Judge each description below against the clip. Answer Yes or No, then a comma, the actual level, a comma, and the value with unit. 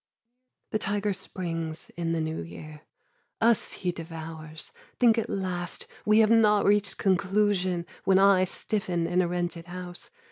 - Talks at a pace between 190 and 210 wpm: No, average, 145 wpm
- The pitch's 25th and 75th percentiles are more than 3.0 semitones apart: Yes, average, 3.5 semitones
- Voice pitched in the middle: Yes, medium, 180 Hz